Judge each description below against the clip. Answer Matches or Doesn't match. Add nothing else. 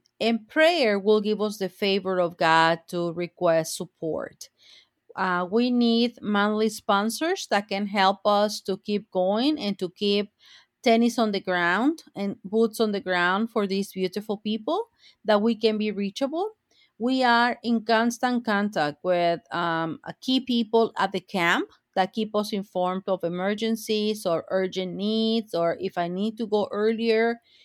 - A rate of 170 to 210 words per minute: Doesn't match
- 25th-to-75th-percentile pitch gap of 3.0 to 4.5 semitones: Matches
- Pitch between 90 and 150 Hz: Doesn't match